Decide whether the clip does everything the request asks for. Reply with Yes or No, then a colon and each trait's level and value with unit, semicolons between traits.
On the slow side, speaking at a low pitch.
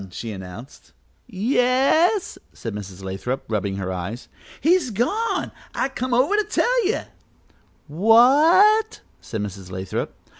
No: slow, 125 wpm; high, 225 Hz